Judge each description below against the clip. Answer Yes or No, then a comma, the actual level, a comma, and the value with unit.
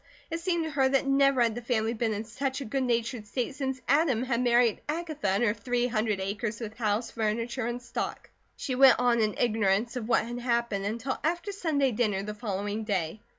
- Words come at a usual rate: No, fast, 210 wpm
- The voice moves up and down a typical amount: Yes, average, 3.6 semitones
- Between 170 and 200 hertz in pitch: No, high, 235 Hz